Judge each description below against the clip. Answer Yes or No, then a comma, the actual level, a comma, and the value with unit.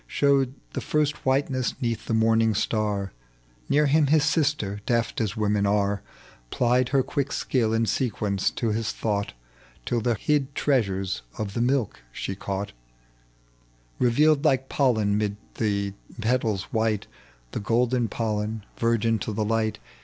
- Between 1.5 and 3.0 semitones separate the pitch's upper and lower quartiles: No, average, 3.9 semitones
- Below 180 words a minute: Yes, average, 145 wpm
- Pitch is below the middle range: Yes, low, 115 Hz